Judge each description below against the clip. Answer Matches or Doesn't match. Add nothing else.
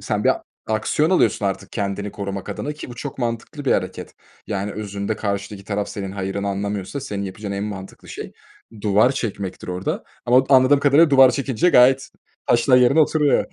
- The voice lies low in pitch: Matches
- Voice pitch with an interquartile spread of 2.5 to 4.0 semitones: Doesn't match